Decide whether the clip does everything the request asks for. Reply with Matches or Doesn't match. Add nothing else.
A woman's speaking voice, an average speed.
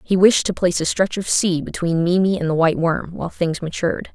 Doesn't match